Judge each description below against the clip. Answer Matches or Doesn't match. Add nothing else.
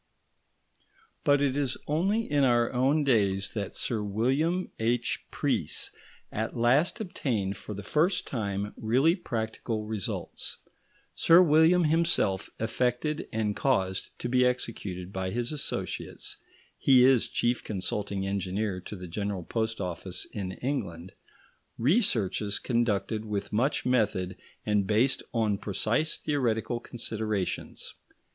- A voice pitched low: Matches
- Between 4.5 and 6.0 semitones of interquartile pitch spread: Matches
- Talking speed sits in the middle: Doesn't match